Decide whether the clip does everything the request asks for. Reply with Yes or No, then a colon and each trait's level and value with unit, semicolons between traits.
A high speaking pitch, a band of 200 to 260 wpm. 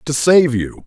No: medium, 140 Hz; fast, 210 wpm